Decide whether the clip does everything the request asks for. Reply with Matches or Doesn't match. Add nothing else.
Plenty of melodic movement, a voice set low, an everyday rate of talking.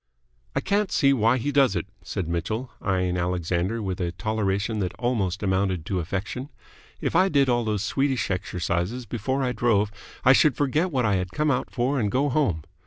Matches